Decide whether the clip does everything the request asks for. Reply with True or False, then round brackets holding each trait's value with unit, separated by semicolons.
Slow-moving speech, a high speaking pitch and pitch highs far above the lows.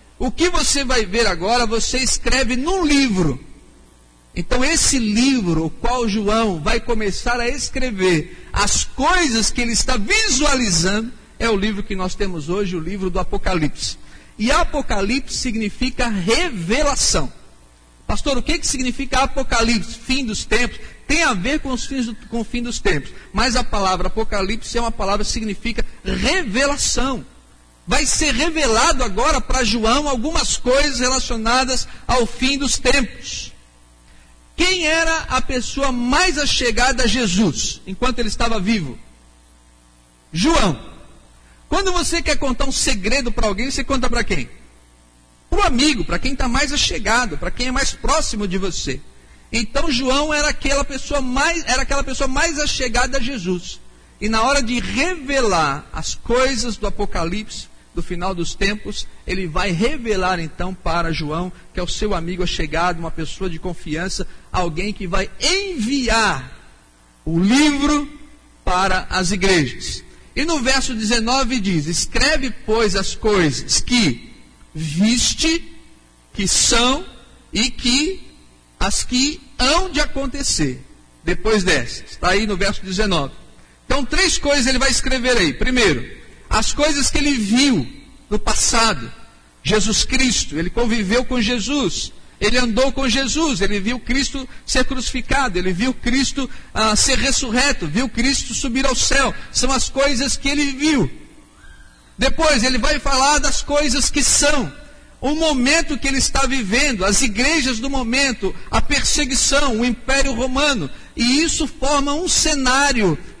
False (145 wpm; 245 Hz; 5.8 semitones)